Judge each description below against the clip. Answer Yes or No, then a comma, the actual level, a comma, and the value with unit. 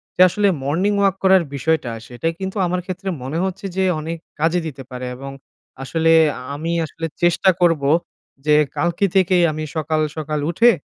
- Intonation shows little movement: No, average, 3.7 semitones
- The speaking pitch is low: No, medium, 165 Hz